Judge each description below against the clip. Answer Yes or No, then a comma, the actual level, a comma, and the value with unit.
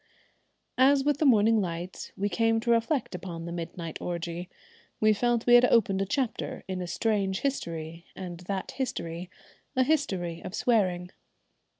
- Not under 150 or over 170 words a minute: Yes, average, 160 wpm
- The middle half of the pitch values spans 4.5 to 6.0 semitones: Yes, wide, 5.5 semitones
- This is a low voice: No, high, 195 Hz